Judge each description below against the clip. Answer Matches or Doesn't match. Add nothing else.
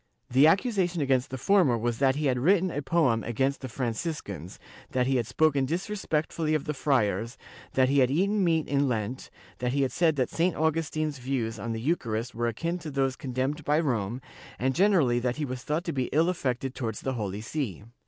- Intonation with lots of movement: Doesn't match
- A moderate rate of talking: Doesn't match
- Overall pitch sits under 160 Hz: Matches